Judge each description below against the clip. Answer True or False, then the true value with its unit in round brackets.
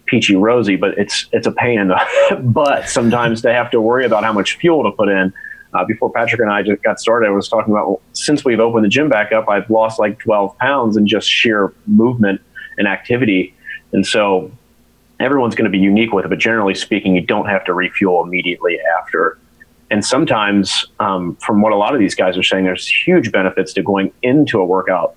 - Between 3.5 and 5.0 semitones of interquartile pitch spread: False (2.8 semitones)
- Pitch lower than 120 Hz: True (105 Hz)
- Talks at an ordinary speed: False (220 wpm)